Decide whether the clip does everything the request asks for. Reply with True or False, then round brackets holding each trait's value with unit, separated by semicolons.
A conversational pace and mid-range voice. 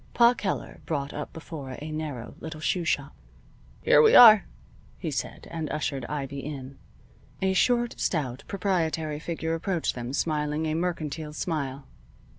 True (145 wpm; 155 Hz)